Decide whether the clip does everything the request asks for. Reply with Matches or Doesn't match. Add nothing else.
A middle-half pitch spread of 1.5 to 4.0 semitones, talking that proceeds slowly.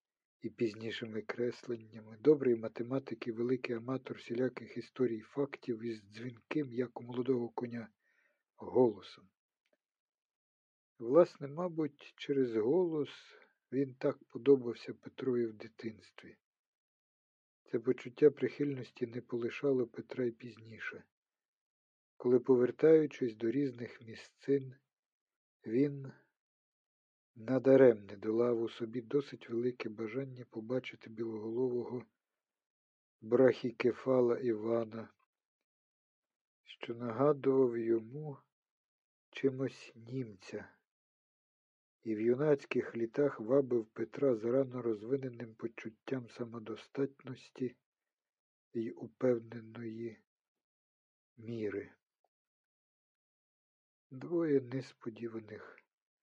Matches